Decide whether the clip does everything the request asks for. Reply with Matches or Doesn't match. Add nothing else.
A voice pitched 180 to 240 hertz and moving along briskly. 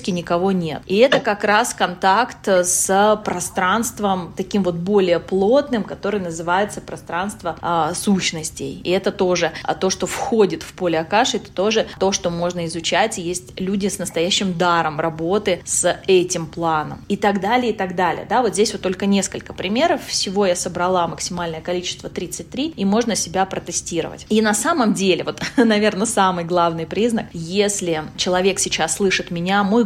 Matches